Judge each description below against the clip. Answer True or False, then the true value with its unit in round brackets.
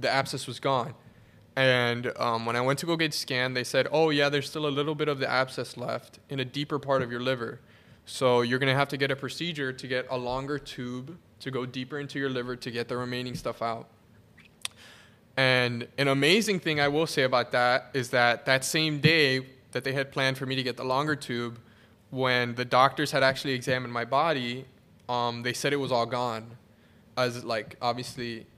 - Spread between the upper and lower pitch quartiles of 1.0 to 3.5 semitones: True (2.4 semitones)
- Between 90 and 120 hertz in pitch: False (130 Hz)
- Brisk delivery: True (215 wpm)